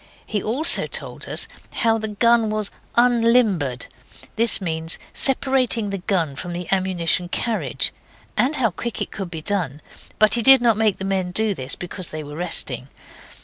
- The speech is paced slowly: No, average, 175 wpm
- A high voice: Yes, high, 200 Hz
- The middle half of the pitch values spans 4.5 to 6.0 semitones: Yes, average, 4.9 semitones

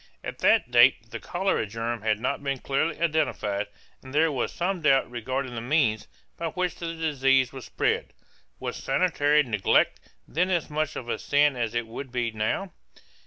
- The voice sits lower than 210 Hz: Yes, low, 135 Hz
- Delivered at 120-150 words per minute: No, average, 175 wpm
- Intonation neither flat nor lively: Yes, average, 4.8 semitones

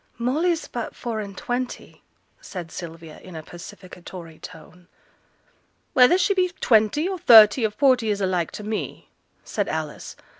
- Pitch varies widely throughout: Yes, wide, 6.1 semitones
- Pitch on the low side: No, high, 215 Hz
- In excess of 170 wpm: No, average, 145 wpm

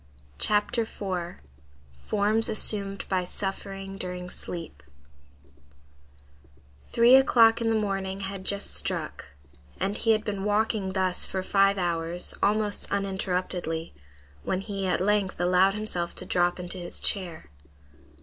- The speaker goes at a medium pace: No, slow, 120 wpm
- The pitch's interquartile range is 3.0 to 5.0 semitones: No, narrow, 2.5 semitones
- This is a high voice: Yes, high, 195 Hz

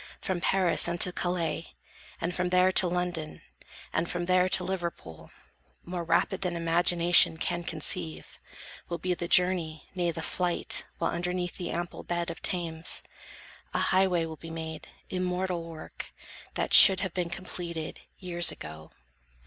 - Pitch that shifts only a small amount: Yes, narrow, 1.5 semitones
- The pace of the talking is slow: No, average, 150 wpm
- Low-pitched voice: No, medium, 175 Hz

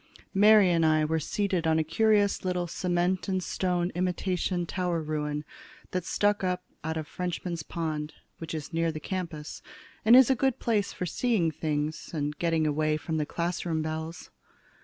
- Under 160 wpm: No, average, 170 wpm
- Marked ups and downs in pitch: No, average, 2.8 semitones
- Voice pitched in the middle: Yes, medium, 170 Hz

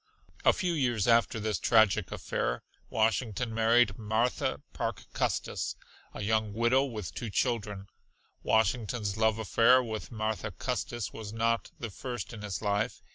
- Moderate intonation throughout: No, narrow, 2.0 semitones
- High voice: No, low, 110 Hz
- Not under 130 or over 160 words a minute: Yes, average, 140 wpm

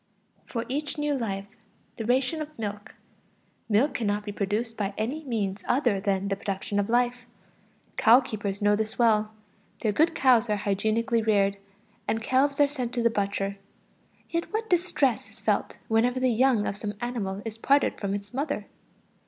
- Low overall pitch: No, high, 225 Hz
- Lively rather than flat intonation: No, average, 4.0 semitones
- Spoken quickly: No, average, 170 wpm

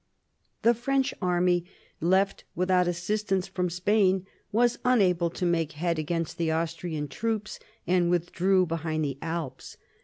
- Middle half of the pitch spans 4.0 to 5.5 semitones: No, average, 2.7 semitones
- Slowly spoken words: Yes, slow, 130 wpm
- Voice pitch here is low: No, medium, 180 Hz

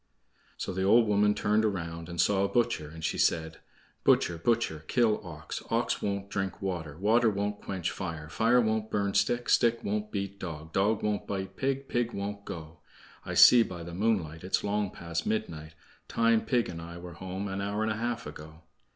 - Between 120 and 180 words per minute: No, average, 195 wpm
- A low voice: Yes, low, 100 Hz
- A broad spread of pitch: No, average, 4.5 semitones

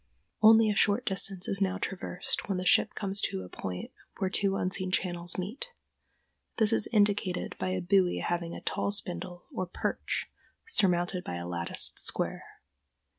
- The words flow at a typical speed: Yes, average, 165 wpm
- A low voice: No, medium, 185 Hz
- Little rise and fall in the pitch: Yes, narrow, 2.3 semitones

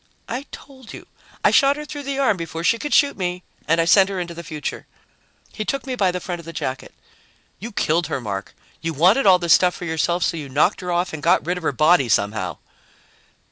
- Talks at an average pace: No, fast, 235 wpm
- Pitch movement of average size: Yes, average, 4.7 semitones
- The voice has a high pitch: No, medium, 175 Hz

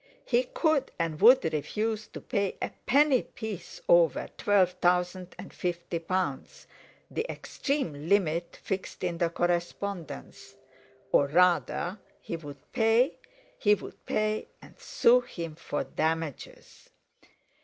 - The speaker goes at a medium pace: No, slow, 120 wpm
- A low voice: No, medium, 185 Hz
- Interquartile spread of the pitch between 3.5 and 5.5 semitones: Yes, average, 4.9 semitones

